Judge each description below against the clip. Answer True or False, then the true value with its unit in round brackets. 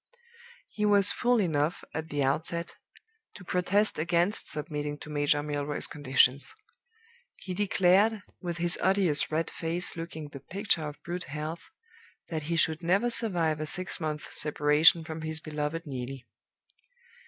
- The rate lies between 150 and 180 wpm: False (140 wpm)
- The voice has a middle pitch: True (160 Hz)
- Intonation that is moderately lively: True (3.3 semitones)